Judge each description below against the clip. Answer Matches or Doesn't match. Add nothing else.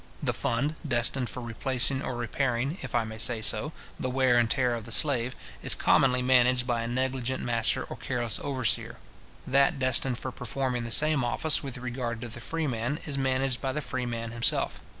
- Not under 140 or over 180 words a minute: Doesn't match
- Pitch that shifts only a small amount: Matches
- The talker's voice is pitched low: Matches